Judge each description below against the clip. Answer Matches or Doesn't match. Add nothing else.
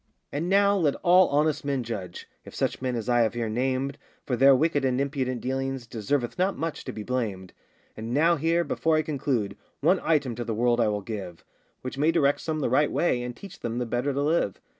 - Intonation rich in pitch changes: Doesn't match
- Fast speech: Matches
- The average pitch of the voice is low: Matches